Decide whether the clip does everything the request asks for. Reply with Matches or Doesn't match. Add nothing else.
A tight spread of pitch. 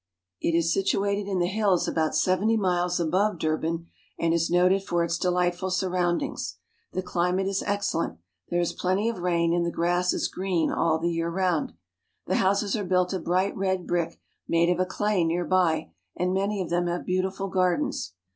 Matches